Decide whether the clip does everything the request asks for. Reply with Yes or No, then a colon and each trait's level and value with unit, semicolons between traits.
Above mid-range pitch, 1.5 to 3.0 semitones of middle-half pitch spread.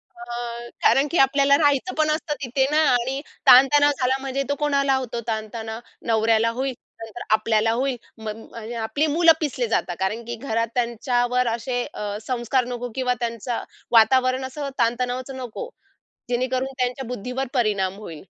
Yes: high, 245 Hz; average, 2.7 semitones